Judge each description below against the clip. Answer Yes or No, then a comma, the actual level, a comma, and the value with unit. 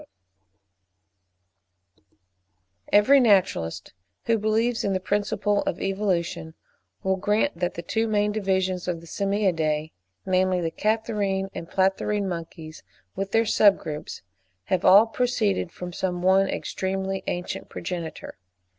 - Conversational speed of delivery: No, slow, 120 wpm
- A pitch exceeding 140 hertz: Yes, high, 190 Hz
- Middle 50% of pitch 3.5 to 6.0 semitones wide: No, average, 2.7 semitones